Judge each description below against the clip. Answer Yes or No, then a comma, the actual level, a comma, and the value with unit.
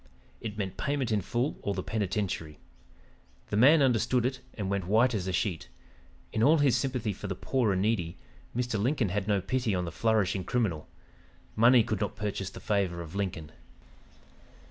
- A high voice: No, low, 105 Hz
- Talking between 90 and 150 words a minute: No, average, 180 wpm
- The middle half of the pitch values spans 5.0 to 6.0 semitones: No, average, 4.4 semitones